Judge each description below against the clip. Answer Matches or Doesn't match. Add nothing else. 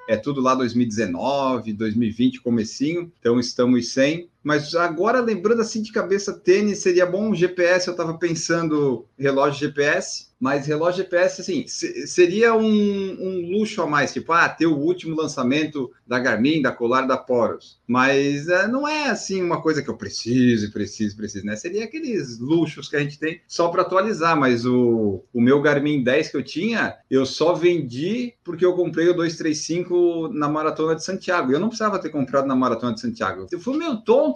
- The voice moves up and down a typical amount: Doesn't match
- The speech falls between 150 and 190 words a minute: Matches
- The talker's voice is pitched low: Doesn't match